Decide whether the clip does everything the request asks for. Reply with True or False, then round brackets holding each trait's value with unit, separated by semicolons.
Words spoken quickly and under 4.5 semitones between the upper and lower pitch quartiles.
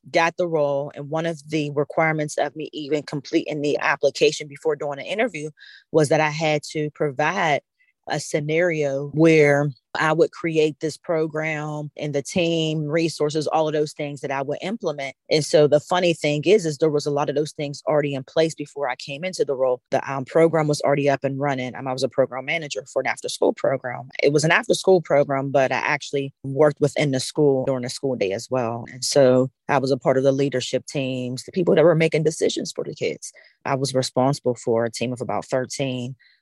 True (220 wpm; 2.6 semitones)